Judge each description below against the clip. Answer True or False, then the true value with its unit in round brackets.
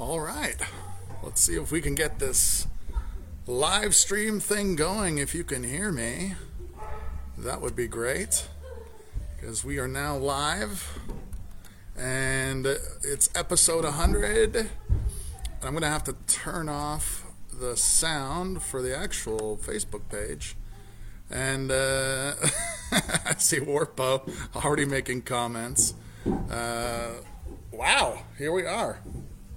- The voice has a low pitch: True (120 Hz)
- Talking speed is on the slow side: True (120 wpm)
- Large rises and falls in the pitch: True (6.9 semitones)